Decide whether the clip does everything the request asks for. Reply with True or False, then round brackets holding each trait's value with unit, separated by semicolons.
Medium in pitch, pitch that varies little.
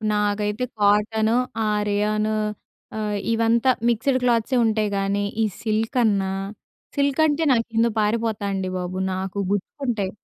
False (215 Hz; 2.1 semitones)